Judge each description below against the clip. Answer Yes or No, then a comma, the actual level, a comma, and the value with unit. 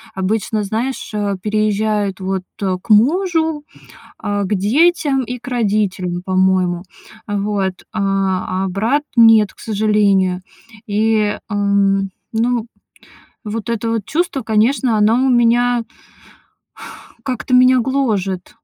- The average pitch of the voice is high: Yes, high, 215 Hz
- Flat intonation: No, average, 3.6 semitones